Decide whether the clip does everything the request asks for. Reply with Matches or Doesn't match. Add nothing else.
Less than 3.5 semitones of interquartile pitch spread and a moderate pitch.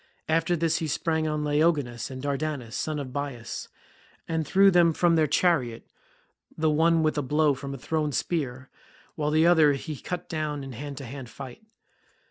Matches